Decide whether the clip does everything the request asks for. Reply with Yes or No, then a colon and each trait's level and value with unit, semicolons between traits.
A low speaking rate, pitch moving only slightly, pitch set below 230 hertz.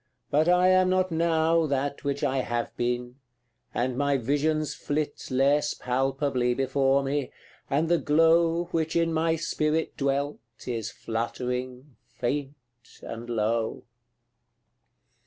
No: slow, 120 wpm; average, 4.2 semitones; medium, 140 Hz